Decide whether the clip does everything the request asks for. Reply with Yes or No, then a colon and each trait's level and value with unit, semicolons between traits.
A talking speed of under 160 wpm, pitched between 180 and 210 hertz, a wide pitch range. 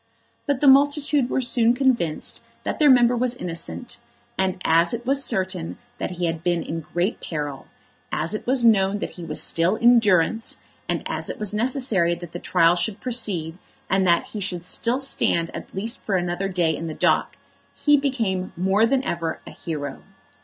No: average, 190 wpm; high, 190 Hz; wide, 6.1 semitones